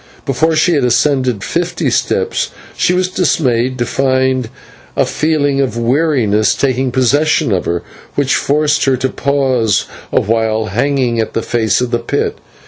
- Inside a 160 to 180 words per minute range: No, average, 150 wpm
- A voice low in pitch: Yes, low, 130 Hz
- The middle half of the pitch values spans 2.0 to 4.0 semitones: Yes, average, 3.4 semitones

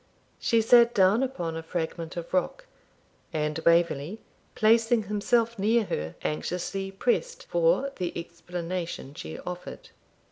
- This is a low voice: No, medium, 185 Hz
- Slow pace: Yes, slow, 120 wpm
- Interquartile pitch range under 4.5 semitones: No, wide, 5.6 semitones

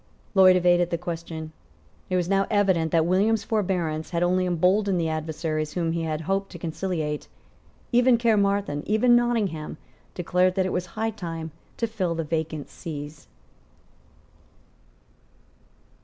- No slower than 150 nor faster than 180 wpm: No, average, 140 wpm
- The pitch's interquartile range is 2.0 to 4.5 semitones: Yes, average, 3.6 semitones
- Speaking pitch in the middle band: Yes, medium, 175 Hz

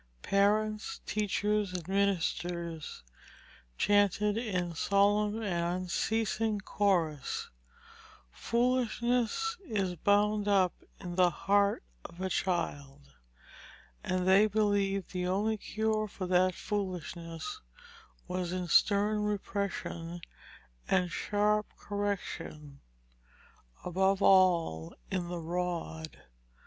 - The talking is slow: Yes, slow, 90 wpm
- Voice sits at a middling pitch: No, high, 195 Hz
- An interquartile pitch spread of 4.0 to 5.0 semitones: No, average, 2.9 semitones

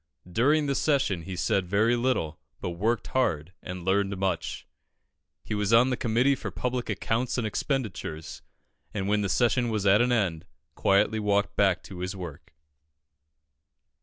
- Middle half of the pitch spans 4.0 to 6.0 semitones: Yes, average, 4.6 semitones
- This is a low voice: Yes, low, 105 Hz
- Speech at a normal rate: Yes, average, 160 wpm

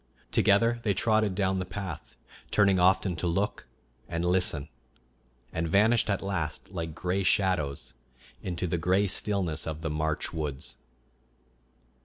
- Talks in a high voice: No, very low, 90 Hz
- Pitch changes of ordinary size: Yes, average, 3.5 semitones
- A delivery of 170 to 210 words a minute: No, slow, 135 wpm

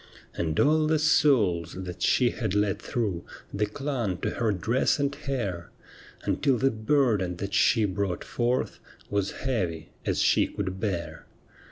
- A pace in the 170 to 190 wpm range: No, average, 150 wpm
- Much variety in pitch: Yes, wide, 6.1 semitones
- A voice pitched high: No, low, 105 Hz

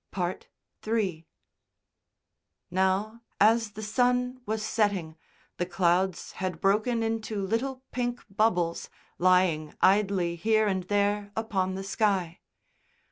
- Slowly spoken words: Yes, slow, 105 wpm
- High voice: Yes, high, 200 Hz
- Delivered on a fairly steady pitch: No, average, 3.2 semitones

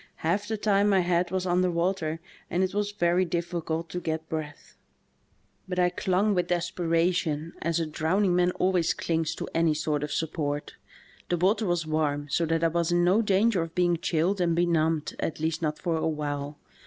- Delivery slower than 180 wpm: No, average, 190 wpm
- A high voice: No, medium, 170 Hz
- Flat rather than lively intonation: Yes, narrow, 2.3 semitones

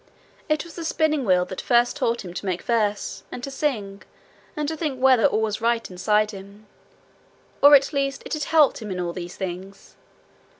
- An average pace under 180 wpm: No, average, 200 wpm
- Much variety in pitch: Yes, wide, 6.0 semitones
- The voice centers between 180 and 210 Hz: No, high, 230 Hz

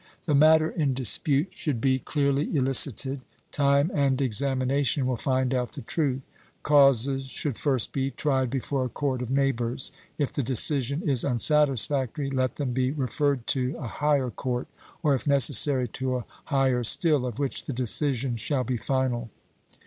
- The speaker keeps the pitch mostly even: Yes, narrow, 2.0 semitones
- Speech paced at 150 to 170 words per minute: Yes, average, 160 wpm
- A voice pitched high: No, low, 135 Hz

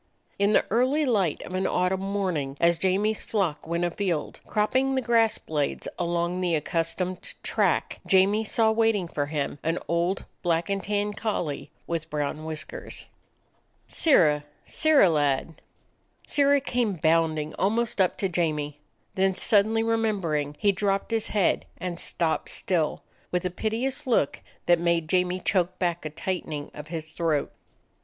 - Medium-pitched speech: Yes, medium, 180 Hz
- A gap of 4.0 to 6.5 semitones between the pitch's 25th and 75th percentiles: Yes, average, 4.5 semitones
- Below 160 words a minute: Yes, average, 150 wpm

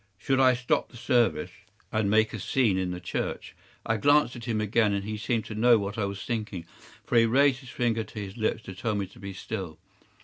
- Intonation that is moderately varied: Yes, average, 3.2 semitones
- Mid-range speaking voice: No, low, 110 Hz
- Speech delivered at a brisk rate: Yes, fast, 235 wpm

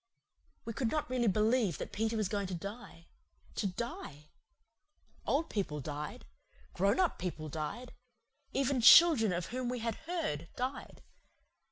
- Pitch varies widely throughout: Yes, wide, 6.2 semitones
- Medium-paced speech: Yes, average, 145 wpm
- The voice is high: Yes, high, 220 Hz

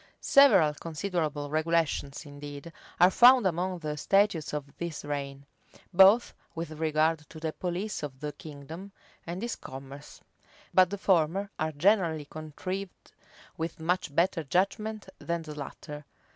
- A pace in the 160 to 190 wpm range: No, slow, 135 wpm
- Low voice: No, medium, 165 Hz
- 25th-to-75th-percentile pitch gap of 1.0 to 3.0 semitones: No, average, 4.0 semitones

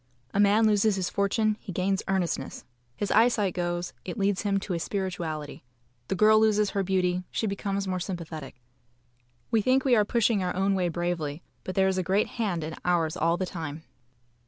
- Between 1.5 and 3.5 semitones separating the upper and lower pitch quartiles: Yes, average, 2.8 semitones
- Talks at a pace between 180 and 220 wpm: Yes, average, 190 wpm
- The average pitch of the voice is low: No, high, 190 Hz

